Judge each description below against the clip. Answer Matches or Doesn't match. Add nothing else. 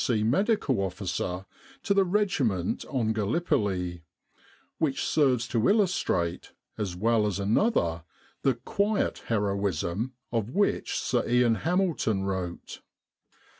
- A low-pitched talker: Matches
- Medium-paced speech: Doesn't match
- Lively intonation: Matches